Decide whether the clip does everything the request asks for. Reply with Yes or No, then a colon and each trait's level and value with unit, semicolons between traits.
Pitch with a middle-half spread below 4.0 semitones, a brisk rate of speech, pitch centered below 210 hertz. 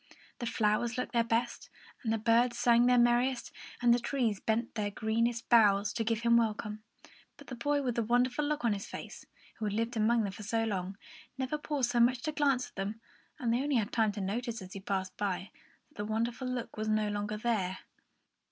No: narrow, 2.4 semitones; fast, 225 wpm; high, 230 Hz